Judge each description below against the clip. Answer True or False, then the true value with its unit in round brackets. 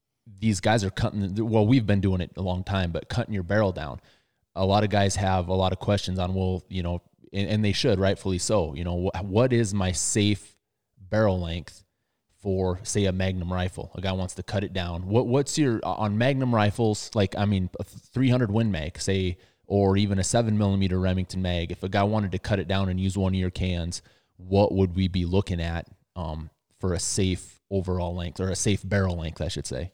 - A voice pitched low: True (95 Hz)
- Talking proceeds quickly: True (225 wpm)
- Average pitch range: False (2.3 semitones)